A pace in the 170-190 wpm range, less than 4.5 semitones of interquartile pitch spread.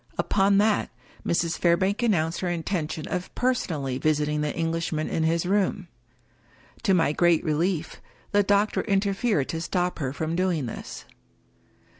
No: average, 145 wpm; average, 3.8 semitones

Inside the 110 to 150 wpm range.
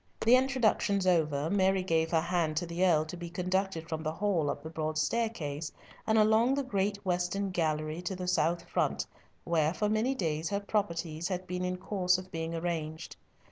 No: average, 190 wpm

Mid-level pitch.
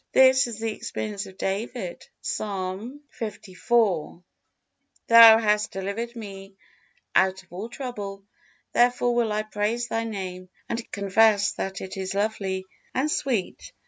No: high, 210 Hz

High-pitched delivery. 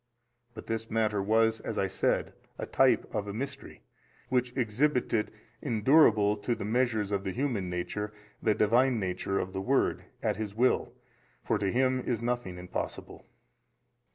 No: low, 110 Hz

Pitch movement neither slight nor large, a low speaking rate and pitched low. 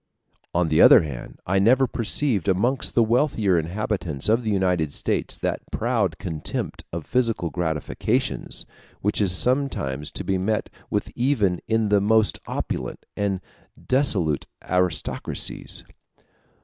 Yes: average, 4.7 semitones; slow, 130 wpm; low, 100 Hz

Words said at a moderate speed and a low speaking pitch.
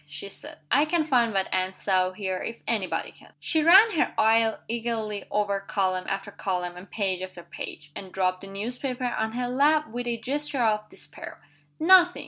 No: average, 190 wpm; high, 215 Hz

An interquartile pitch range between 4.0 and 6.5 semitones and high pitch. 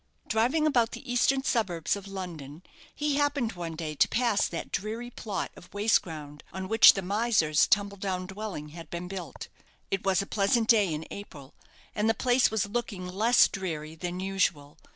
Yes: average, 4.7 semitones; high, 195 Hz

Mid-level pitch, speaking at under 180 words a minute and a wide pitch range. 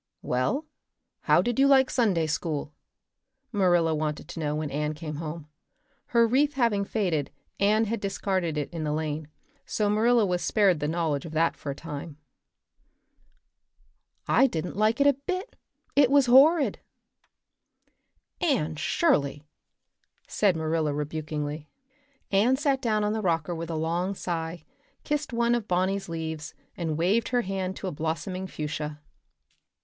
Yes: medium, 175 Hz; average, 150 wpm; wide, 6.4 semitones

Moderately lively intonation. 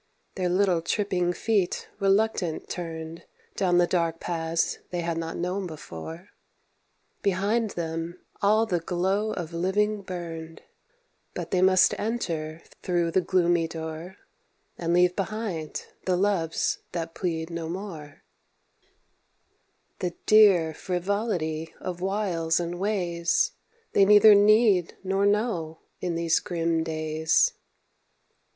Yes: average, 3.1 semitones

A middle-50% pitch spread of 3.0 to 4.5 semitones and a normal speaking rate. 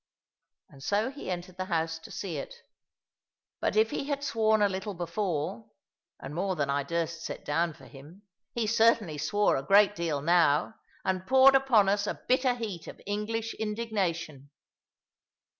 No: average, 5.1 semitones; average, 165 wpm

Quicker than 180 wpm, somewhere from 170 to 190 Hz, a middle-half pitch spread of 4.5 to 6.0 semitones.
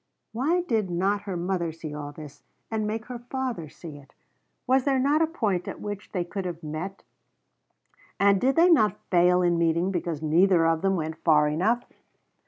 Yes: average, 190 wpm; medium, 185 Hz; average, 5.2 semitones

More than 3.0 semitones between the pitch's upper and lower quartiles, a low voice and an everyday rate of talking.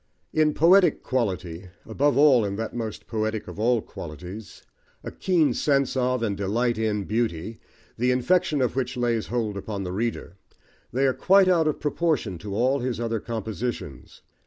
Yes: average, 4.3 semitones; low, 115 Hz; average, 165 wpm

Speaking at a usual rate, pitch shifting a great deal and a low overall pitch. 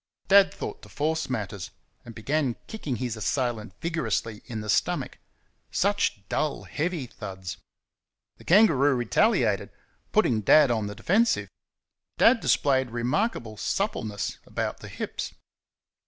No: slow, 125 wpm; wide, 6.7 semitones; low, 125 Hz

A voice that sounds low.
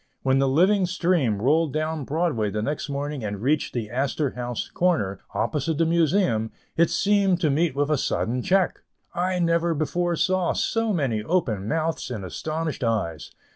No: medium, 150 Hz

